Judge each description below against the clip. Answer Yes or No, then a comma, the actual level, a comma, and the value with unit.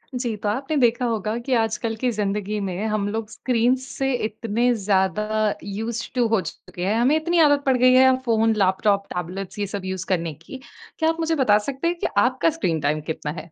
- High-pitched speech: Yes, high, 225 Hz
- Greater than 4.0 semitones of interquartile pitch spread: Yes, average, 4.5 semitones